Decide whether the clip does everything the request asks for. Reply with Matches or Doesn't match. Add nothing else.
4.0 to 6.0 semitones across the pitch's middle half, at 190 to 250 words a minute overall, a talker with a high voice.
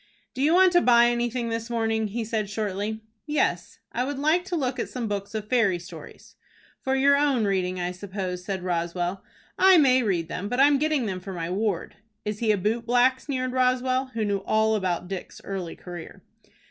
Matches